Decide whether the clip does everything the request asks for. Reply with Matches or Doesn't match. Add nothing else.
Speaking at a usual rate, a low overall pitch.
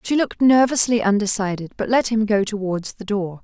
Doesn't match